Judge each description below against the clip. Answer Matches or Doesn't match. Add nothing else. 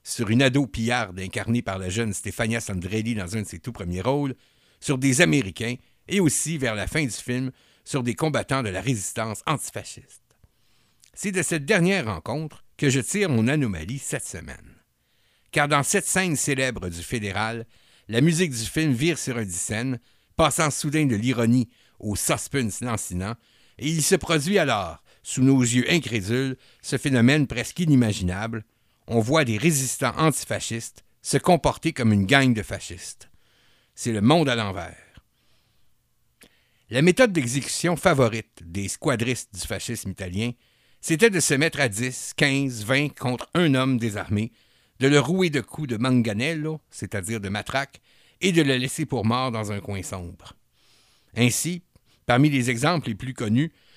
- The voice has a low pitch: Matches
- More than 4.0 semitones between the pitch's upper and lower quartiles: Matches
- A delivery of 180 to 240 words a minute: Doesn't match